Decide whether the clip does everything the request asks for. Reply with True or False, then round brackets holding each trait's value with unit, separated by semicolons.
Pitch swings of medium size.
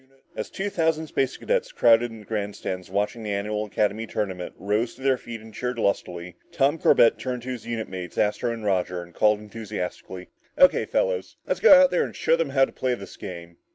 True (4.7 semitones)